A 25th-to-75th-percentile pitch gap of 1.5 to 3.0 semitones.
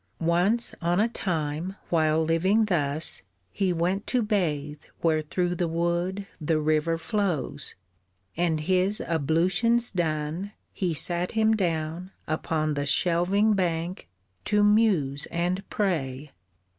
No: average, 3.7 semitones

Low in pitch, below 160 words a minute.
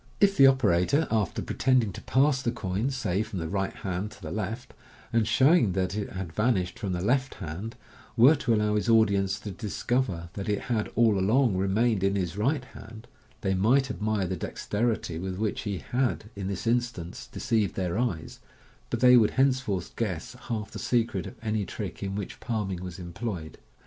No: low, 105 Hz; average, 190 wpm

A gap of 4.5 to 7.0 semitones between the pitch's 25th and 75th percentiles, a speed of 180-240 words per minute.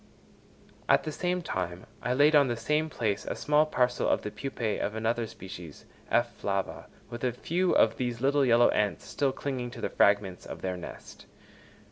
Yes: average, 5.3 semitones; average, 185 wpm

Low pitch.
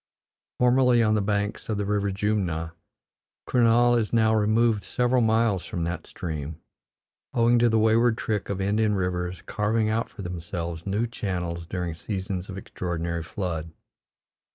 Yes: low, 100 Hz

